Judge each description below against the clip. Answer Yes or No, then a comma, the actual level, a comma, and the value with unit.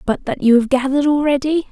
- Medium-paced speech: No, fast, 210 wpm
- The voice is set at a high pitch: Yes, very high, 275 Hz